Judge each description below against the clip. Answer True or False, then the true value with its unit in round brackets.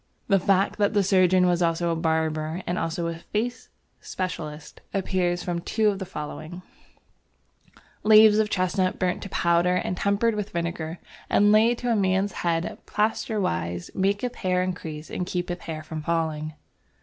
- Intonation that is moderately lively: True (3.3 semitones)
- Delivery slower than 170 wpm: True (155 wpm)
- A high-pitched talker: False (180 Hz)